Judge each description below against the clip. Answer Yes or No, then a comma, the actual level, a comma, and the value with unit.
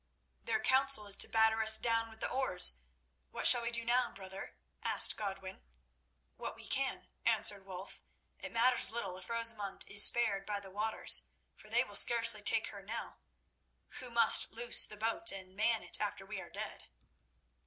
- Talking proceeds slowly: No, average, 175 wpm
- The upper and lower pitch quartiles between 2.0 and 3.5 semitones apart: Yes, average, 3.0 semitones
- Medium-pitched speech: No, high, 220 Hz